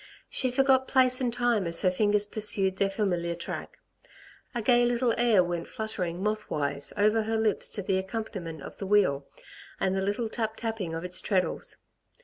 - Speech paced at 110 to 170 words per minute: No, average, 180 wpm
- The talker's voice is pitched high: Yes, high, 205 Hz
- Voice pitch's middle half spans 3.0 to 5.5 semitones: Yes, average, 3.8 semitones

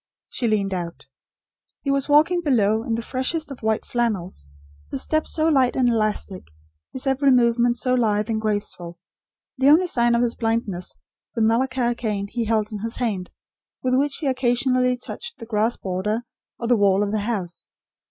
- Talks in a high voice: Yes, high, 235 Hz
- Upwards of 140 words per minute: Yes, average, 180 wpm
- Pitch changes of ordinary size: Yes, average, 3.5 semitones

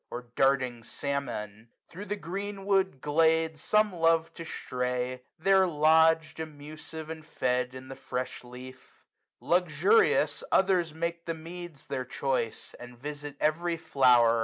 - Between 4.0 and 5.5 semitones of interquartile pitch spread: Yes, average, 4.7 semitones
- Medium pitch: Yes, medium, 155 Hz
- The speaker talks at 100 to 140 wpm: Yes, slow, 135 wpm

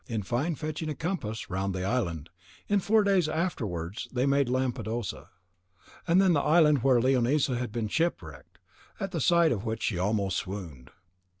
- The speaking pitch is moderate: No, low, 125 Hz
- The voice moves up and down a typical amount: No, wide, 7.6 semitones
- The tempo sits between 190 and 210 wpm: No, average, 165 wpm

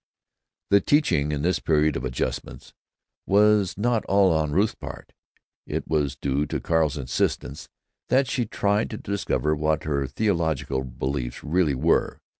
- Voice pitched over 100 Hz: No, very low, 80 Hz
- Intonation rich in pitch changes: Yes, wide, 6.2 semitones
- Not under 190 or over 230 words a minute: No, average, 145 wpm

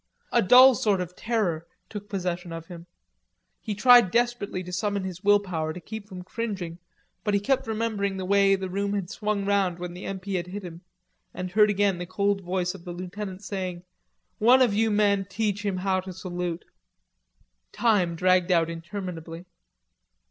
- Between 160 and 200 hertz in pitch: Yes, high, 190 Hz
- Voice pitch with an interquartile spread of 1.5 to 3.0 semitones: Yes, narrow, 2.4 semitones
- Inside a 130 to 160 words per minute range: No, average, 180 wpm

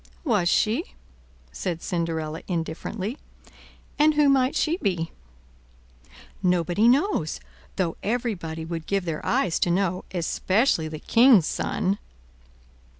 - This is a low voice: No, medium, 185 Hz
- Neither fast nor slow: No, slow, 110 wpm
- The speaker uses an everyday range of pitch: No, wide, 6.3 semitones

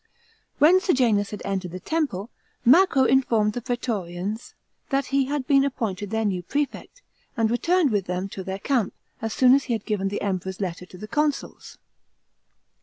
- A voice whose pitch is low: No, high, 225 Hz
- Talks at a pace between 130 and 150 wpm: No, average, 175 wpm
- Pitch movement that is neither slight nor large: No, wide, 5.8 semitones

